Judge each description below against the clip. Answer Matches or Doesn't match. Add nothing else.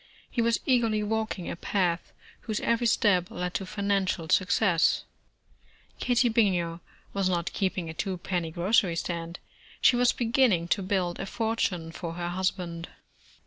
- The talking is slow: Doesn't match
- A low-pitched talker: Doesn't match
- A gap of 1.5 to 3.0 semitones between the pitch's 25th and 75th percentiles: Doesn't match